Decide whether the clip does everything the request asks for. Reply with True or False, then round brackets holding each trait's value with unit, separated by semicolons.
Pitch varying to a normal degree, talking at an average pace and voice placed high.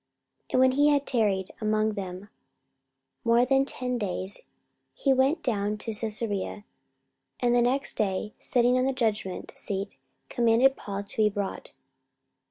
True (3.9 semitones; 150 wpm; 225 Hz)